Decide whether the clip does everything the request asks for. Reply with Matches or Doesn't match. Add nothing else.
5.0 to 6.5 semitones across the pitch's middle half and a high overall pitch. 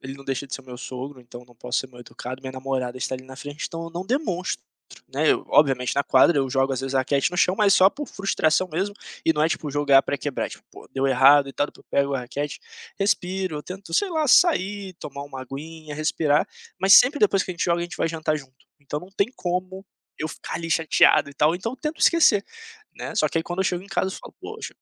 Doesn't match